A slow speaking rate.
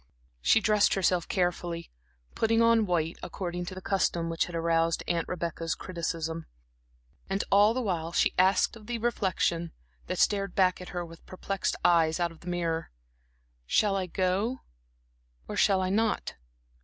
No: average, 160 wpm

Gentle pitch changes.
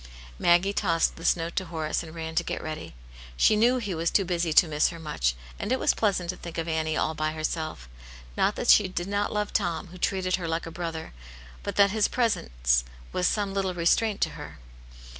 No: average, 3.6 semitones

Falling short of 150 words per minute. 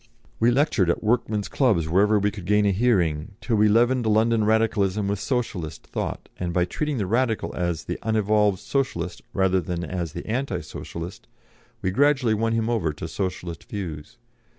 No: average, 175 wpm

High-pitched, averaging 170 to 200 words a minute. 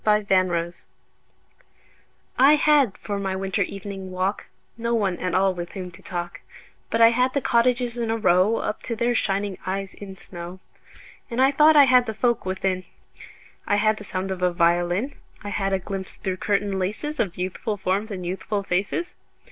Yes: high, 200 Hz; average, 185 wpm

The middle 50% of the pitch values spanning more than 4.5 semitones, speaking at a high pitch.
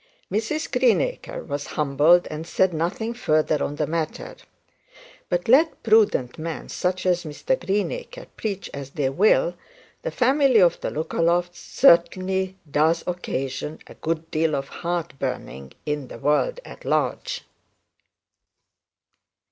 No: wide, 5.4 semitones; medium, 170 Hz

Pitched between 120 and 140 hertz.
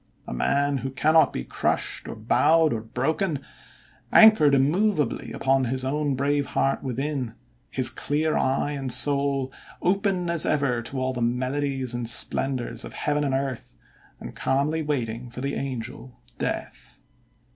Yes: low, 135 Hz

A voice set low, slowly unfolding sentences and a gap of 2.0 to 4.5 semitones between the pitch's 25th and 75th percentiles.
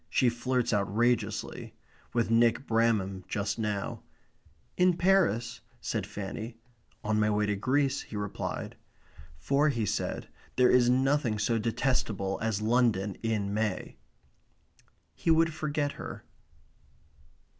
Yes: low, 115 Hz; slow, 120 wpm; average, 3.6 semitones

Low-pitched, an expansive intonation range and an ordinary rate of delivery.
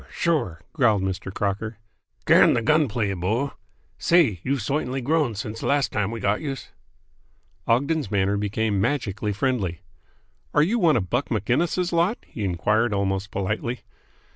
Yes: low, 115 Hz; wide, 6.0 semitones; average, 150 wpm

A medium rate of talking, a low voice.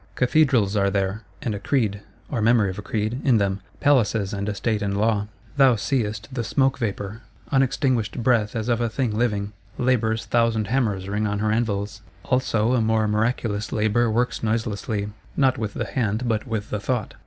Yes: average, 185 wpm; low, 110 Hz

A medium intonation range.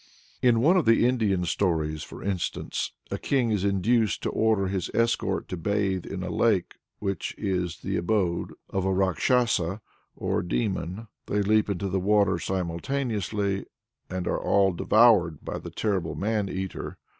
Yes: average, 3.3 semitones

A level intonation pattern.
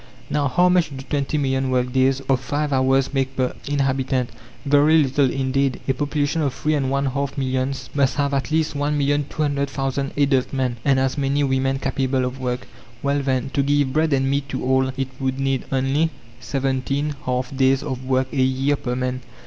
Yes: narrow, 1.4 semitones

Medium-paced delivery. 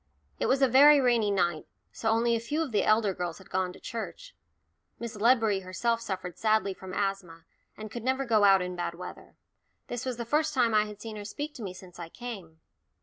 No: fast, 220 wpm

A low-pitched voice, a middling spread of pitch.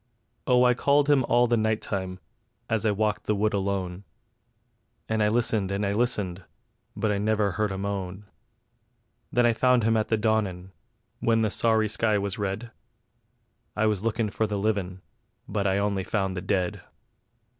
No: low, 105 Hz; narrow, 2.3 semitones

